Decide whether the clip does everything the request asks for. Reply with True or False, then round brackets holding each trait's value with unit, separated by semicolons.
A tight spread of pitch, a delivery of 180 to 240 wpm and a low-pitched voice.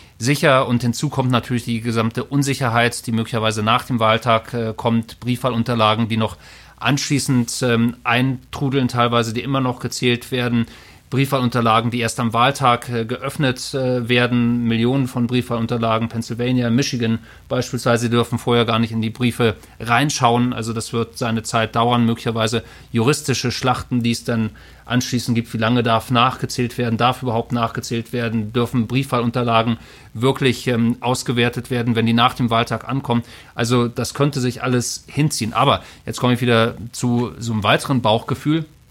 False (1.5 semitones; 155 wpm; 120 Hz)